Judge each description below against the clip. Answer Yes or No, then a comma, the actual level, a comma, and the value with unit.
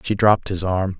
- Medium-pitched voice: No, very low, 95 Hz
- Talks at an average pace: No, fast, 240 wpm